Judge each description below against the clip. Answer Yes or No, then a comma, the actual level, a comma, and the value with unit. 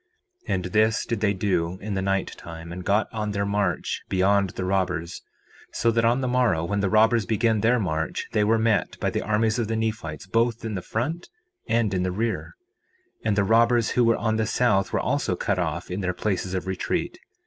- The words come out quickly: Yes, fast, 220 wpm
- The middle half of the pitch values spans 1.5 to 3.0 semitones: No, average, 3.4 semitones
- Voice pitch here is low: Yes, low, 105 Hz